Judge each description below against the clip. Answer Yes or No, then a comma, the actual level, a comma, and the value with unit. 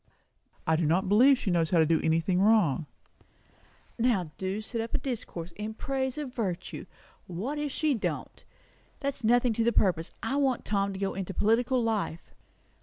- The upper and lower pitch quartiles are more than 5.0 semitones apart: Yes, wide, 5.6 semitones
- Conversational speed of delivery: Yes, average, 180 wpm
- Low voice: No, high, 210 Hz